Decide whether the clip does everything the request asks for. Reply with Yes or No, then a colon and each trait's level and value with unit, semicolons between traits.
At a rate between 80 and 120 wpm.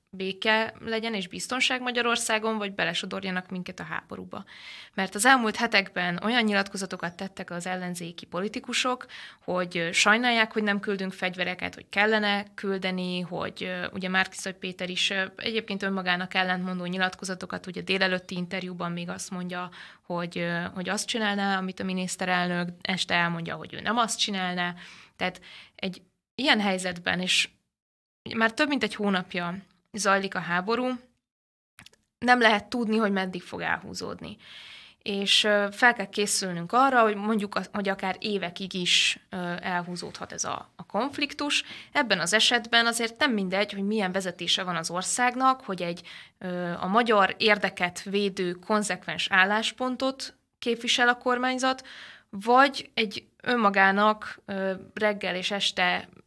No: average, 130 wpm